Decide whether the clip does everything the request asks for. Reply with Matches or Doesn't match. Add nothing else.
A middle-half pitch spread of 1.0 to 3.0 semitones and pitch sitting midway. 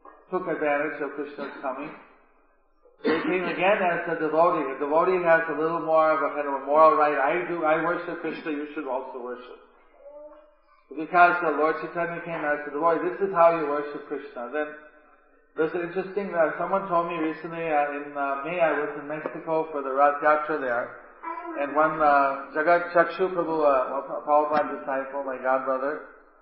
Matches